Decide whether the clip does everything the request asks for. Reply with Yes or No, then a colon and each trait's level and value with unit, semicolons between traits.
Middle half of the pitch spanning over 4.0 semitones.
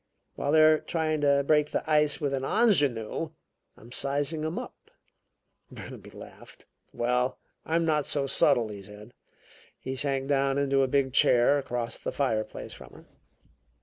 No: average, 3.2 semitones